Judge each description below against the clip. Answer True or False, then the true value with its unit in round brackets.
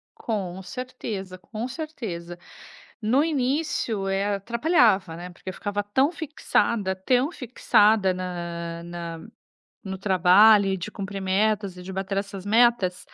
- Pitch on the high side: True (200 Hz)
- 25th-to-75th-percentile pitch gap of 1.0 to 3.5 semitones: False (4.2 semitones)